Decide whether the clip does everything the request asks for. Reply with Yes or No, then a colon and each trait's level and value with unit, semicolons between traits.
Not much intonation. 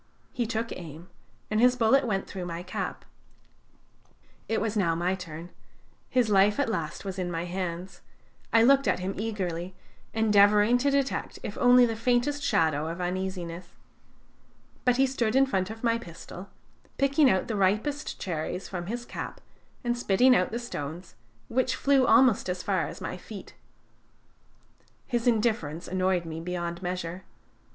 No: average, 5.2 semitones